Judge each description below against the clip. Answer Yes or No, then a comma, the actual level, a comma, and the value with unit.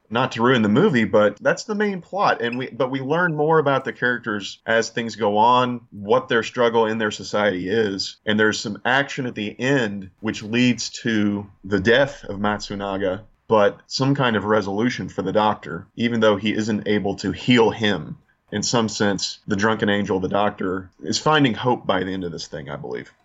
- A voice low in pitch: Yes, low, 110 Hz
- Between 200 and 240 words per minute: Yes, fast, 205 wpm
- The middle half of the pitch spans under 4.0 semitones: Yes, average, 3.5 semitones